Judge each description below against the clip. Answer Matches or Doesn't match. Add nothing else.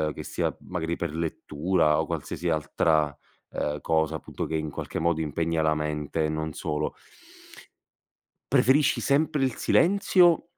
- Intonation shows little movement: Doesn't match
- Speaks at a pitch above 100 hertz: Doesn't match